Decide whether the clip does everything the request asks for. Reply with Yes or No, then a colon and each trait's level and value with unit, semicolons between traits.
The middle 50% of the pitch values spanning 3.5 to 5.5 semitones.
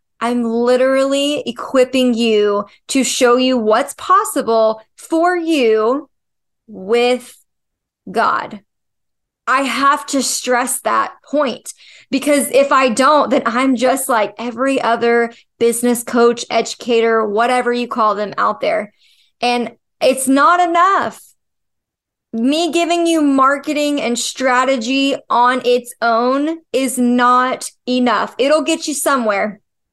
No: average, 2.8 semitones